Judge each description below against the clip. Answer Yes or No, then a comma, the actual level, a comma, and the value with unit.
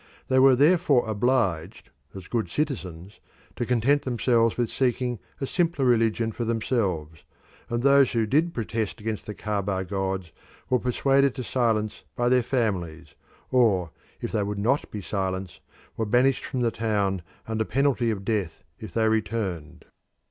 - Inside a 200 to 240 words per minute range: No, average, 155 wpm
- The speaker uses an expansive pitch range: No, average, 4.2 semitones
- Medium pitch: No, low, 115 Hz